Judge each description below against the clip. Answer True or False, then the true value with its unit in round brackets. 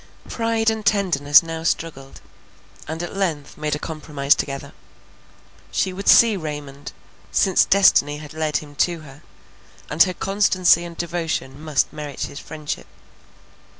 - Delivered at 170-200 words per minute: False (140 wpm)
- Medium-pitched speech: True (160 Hz)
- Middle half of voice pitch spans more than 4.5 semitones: False (4.0 semitones)